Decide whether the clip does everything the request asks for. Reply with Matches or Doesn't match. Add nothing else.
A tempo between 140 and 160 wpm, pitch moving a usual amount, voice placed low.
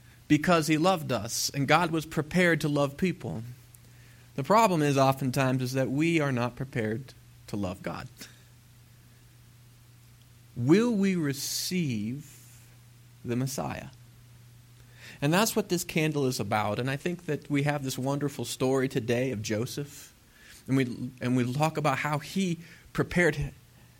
Matches